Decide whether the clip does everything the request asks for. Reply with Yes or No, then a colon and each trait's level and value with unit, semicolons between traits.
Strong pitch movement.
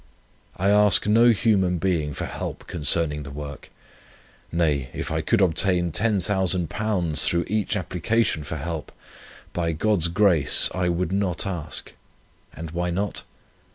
No: average, 3.8 semitones